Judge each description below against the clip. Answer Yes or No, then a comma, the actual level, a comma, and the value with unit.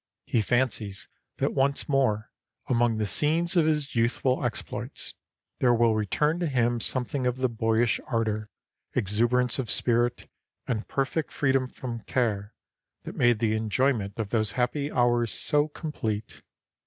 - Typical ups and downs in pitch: Yes, average, 3.2 semitones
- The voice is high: No, low, 120 Hz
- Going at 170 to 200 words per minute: No, average, 140 wpm